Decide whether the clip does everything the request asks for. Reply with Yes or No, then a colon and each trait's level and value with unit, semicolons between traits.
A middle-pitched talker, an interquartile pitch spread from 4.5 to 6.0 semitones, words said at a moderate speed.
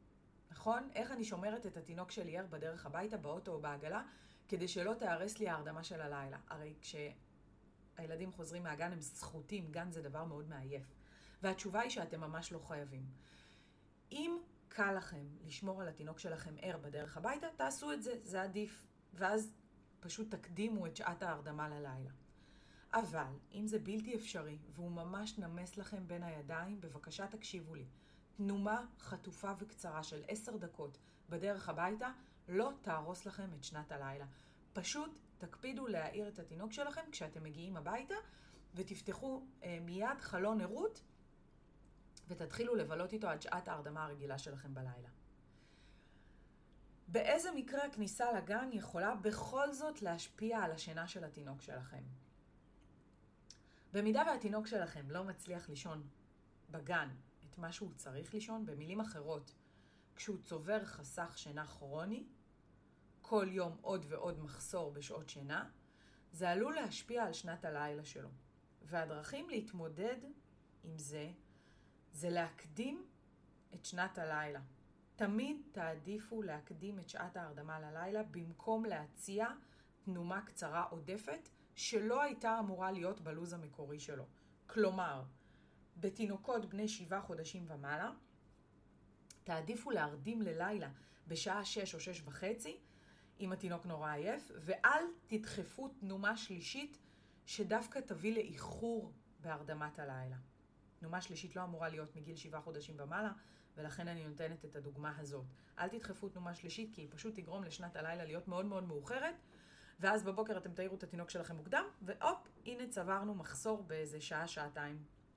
Yes: medium, 180 Hz; wide, 5.6 semitones; average, 130 wpm